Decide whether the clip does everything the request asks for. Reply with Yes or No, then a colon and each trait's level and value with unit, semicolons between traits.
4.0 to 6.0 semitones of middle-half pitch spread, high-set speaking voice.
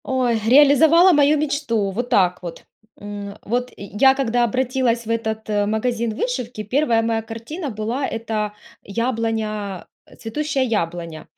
No: average, 3.6 semitones; high, 230 Hz